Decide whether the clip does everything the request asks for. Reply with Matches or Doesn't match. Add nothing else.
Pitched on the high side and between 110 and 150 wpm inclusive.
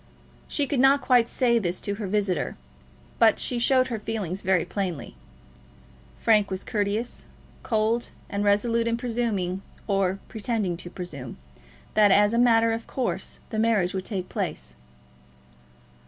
Matches